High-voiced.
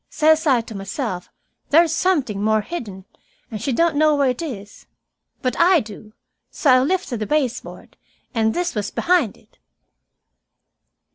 Yes: very high, 255 Hz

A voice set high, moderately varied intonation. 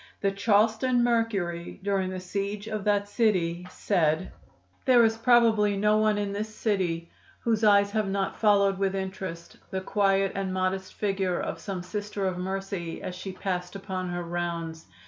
No: high, 195 Hz; narrow, 2.3 semitones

